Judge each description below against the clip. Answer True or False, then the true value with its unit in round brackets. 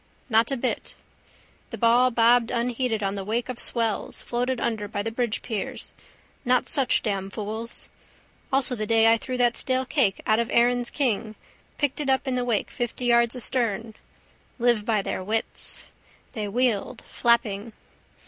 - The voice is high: True (235 Hz)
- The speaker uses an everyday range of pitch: False (2.3 semitones)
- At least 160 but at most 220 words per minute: True (165 wpm)